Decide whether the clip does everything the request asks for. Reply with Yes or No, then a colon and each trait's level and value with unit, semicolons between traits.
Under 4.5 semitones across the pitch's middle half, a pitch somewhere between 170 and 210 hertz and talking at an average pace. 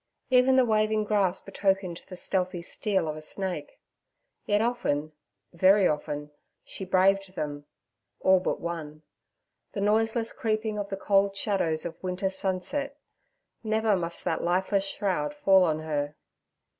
No: average, 4.0 semitones; high, 190 Hz; slow, 130 wpm